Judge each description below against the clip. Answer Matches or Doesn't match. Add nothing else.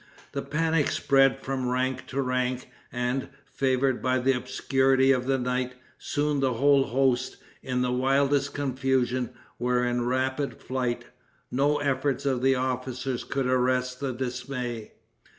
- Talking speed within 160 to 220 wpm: Doesn't match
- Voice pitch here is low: Matches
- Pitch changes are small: Matches